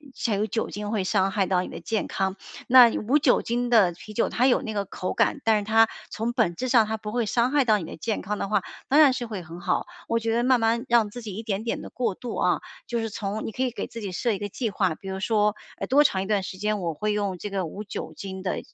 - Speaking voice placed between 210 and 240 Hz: Yes, high, 215 Hz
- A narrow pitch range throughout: No, average, 3.2 semitones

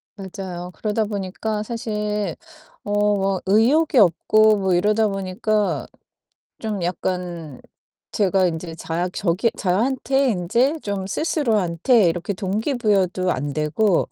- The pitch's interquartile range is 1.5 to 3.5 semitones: Yes, average, 3.2 semitones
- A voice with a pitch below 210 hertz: Yes, high, 200 Hz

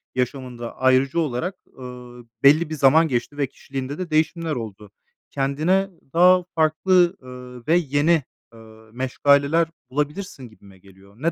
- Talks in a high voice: No, medium, 140 Hz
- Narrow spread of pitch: No, average, 4.6 semitones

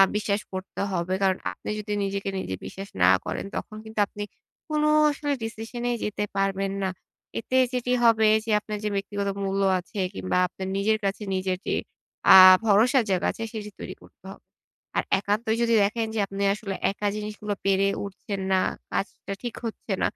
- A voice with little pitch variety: Yes, narrow, 2.1 semitones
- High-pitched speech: Yes, high, 205 Hz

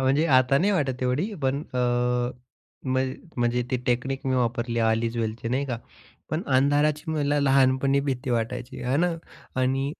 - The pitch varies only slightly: Yes, narrow, 2.3 semitones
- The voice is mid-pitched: No, low, 130 Hz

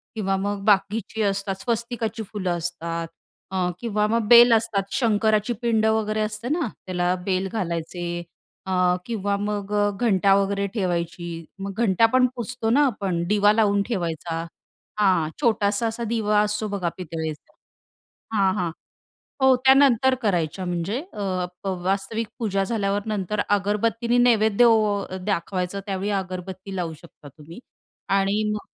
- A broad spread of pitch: No, average, 3.0 semitones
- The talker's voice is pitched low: No, high, 200 Hz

